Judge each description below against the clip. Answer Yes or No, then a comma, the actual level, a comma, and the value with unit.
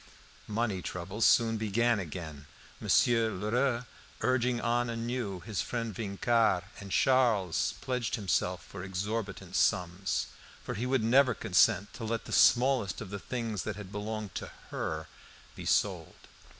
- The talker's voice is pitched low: Yes, low, 110 Hz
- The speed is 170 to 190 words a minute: No, average, 140 wpm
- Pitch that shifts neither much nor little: Yes, average, 3.6 semitones